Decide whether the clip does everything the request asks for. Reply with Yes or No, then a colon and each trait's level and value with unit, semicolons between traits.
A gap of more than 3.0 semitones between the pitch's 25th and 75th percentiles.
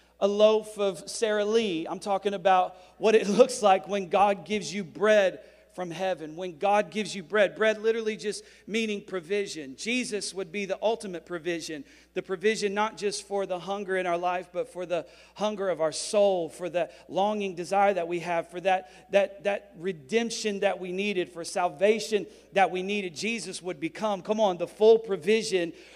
No: narrow, 2.5 semitones